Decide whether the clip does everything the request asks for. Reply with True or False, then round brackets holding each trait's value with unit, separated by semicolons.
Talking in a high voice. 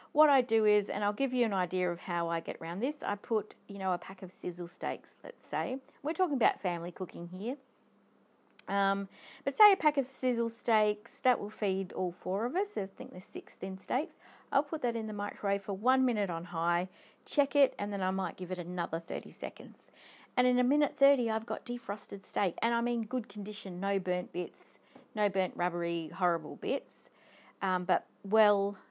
True (205 Hz)